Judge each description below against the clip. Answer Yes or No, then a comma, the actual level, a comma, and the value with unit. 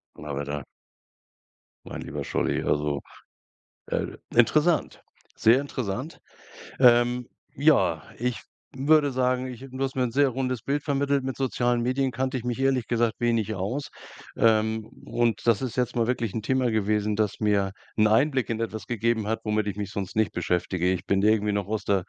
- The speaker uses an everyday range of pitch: Yes, average, 3.5 semitones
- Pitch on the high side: No, low, 115 Hz